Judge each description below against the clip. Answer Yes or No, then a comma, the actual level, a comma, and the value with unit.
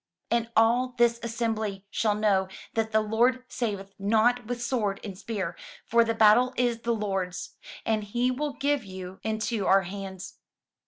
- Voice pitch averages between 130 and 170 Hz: No, high, 220 Hz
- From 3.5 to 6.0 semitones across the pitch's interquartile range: No, average, 3.0 semitones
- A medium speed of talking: Yes, average, 160 wpm